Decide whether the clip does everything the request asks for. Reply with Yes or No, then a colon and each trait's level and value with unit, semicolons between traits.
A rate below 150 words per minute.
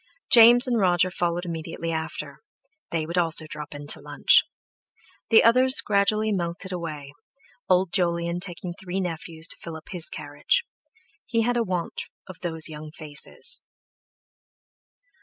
Yes: average, 140 wpm